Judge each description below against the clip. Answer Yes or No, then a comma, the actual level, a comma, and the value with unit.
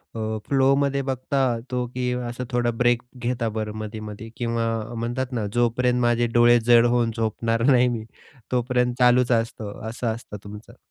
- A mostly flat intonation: Yes, narrow, 1.5 semitones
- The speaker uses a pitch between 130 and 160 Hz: No, low, 120 Hz